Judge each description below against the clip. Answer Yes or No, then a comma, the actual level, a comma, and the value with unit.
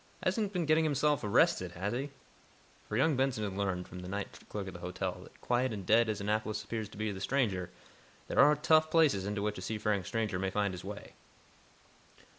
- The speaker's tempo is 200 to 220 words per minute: Yes, fast, 205 wpm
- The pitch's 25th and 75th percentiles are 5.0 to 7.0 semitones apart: Yes, wide, 5.6 semitones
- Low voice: Yes, low, 105 Hz